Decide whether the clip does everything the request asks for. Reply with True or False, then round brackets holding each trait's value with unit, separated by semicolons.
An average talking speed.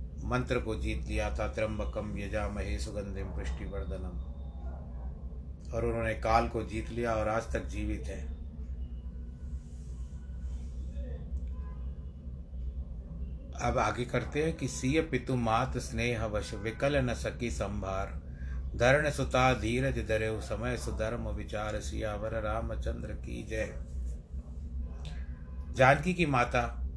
False (105 wpm)